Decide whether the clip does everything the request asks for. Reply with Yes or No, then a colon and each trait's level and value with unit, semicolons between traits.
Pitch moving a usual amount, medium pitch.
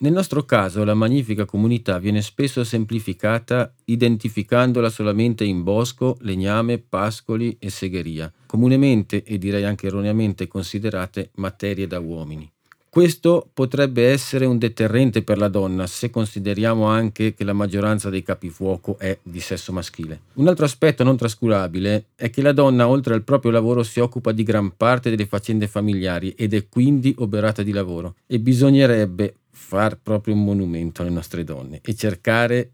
No: average, 3.5 semitones; low, 110 Hz